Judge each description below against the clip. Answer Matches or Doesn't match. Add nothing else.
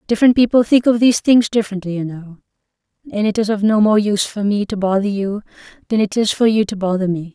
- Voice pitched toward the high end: Matches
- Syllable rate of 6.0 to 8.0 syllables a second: Matches